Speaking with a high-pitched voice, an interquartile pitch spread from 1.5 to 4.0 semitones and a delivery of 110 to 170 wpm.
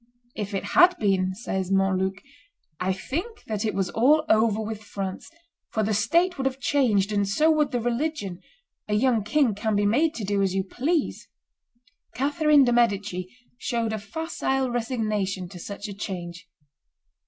No: high, 215 Hz; average, 5.3 semitones; average, 165 wpm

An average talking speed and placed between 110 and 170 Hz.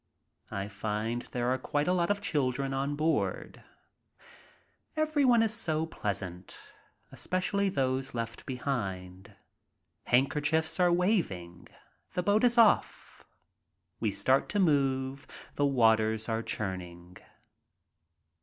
No: slow, 110 wpm; low, 135 Hz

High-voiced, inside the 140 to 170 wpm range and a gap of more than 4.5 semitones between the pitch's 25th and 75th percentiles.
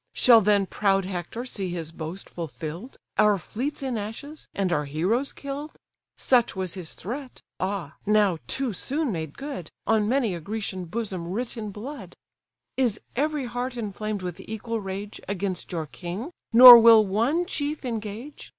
Yes: high, 210 Hz; average, 160 wpm; average, 5.1 semitones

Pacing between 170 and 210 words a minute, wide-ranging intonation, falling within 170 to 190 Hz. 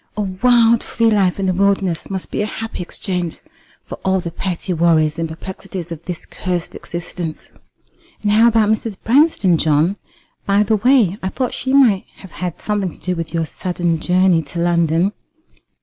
No: average, 180 wpm; average, 3.6 semitones; medium, 185 Hz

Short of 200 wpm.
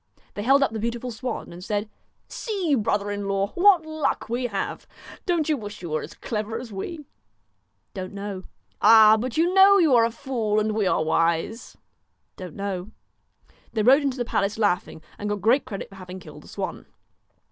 No: fast, 205 wpm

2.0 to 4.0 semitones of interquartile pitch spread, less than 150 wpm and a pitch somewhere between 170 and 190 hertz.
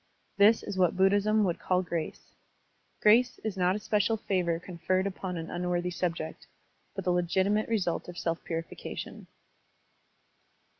Yes: average, 2.7 semitones; average, 140 wpm; medium, 185 Hz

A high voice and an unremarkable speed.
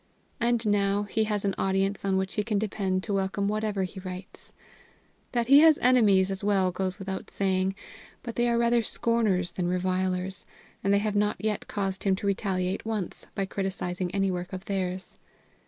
Yes: high, 195 Hz; average, 185 wpm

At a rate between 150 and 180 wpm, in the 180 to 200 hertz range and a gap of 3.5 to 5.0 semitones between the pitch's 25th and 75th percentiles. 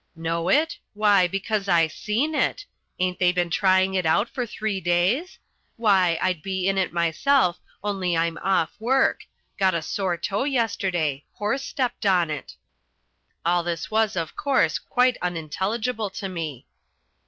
Yes: average, 155 wpm; high, 190 Hz; average, 4.1 semitones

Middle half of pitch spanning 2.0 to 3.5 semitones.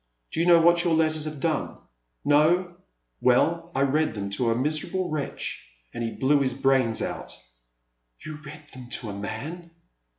No: average, 5.0 semitones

